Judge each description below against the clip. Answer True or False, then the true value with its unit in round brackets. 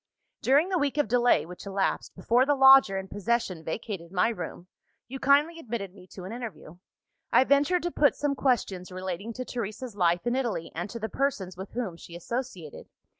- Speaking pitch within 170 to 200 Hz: False (225 Hz)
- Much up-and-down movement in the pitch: True (6.3 semitones)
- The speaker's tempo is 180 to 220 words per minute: True (190 wpm)